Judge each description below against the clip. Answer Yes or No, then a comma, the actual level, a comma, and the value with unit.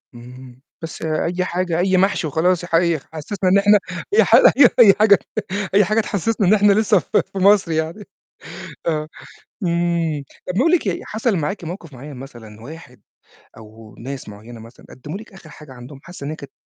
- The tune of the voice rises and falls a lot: Yes, wide, 6.0 semitones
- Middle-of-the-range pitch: Yes, medium, 170 Hz